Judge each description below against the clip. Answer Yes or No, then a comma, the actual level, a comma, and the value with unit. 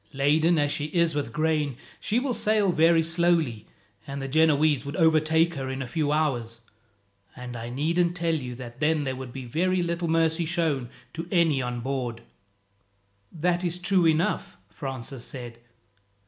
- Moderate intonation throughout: Yes, average, 4.2 semitones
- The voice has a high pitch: No, medium, 155 Hz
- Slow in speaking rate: No, average, 165 wpm